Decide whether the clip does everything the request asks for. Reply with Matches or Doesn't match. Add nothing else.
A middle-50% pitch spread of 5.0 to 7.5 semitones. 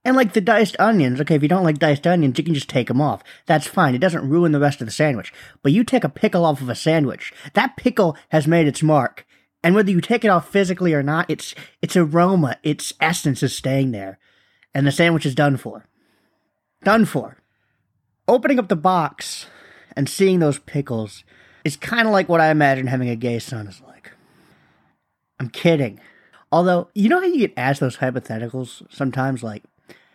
Matches